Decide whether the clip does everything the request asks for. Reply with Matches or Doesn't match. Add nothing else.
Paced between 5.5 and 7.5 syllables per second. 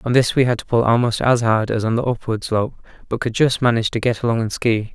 Matches